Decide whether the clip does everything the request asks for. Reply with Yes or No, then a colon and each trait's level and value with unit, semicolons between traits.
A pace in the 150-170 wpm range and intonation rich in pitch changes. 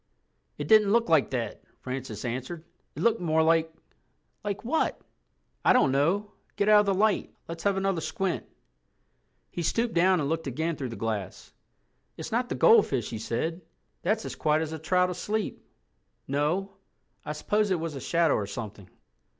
Yes: average, 165 wpm; wide, 6.3 semitones